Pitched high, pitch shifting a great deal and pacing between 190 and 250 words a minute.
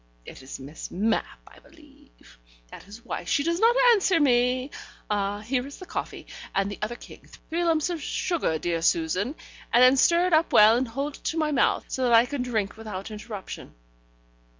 Yes: high, 245 Hz; wide, 6.6 semitones; average, 195 wpm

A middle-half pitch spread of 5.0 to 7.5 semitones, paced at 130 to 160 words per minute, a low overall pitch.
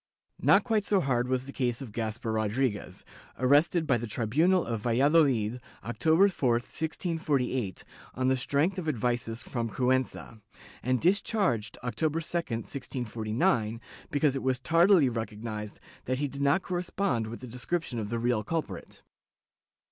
Yes: wide, 5.5 semitones; average, 150 wpm; low, 130 Hz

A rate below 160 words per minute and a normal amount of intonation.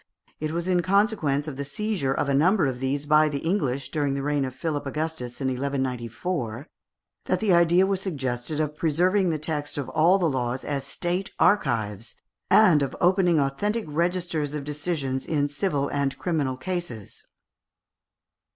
No: average, 165 wpm; average, 4.4 semitones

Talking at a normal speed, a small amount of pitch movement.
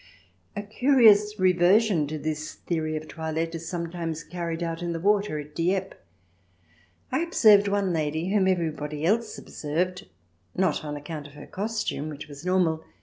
No: average, 160 wpm; average, 3.9 semitones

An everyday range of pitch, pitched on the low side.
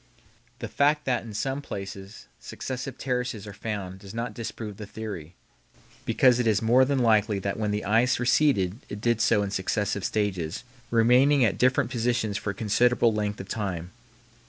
Yes: average, 3.4 semitones; low, 110 Hz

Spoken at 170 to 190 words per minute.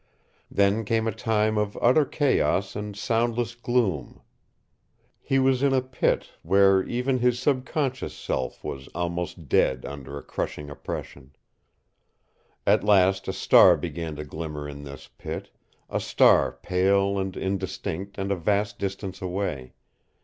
No: average, 140 wpm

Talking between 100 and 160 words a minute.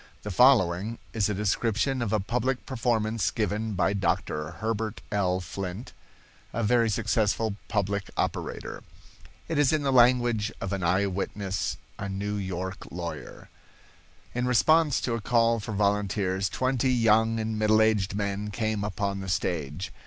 Yes: average, 145 wpm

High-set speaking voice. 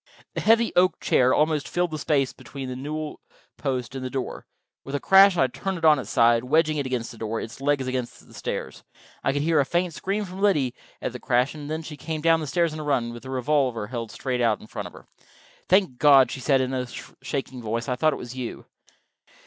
No: low, 135 Hz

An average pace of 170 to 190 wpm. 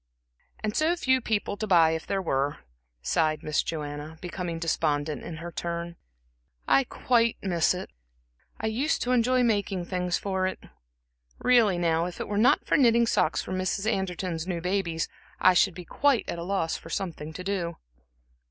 Yes: average, 175 wpm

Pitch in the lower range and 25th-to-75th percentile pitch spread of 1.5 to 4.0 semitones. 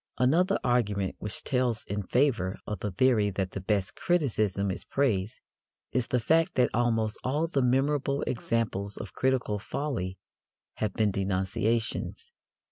No: low, 115 Hz; average, 4.7 semitones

